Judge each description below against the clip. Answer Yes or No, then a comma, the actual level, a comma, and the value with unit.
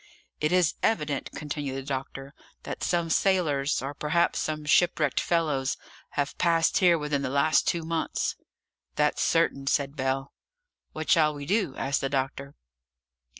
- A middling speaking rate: Yes, average, 150 wpm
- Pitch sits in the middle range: Yes, medium, 150 Hz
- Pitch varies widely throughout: No, average, 3.1 semitones